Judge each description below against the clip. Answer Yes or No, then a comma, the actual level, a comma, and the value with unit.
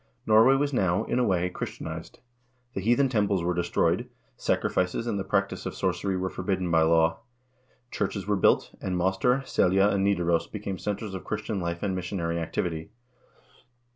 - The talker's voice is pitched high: No, very low, 95 Hz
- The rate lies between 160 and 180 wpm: Yes, average, 170 wpm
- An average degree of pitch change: Yes, average, 3.0 semitones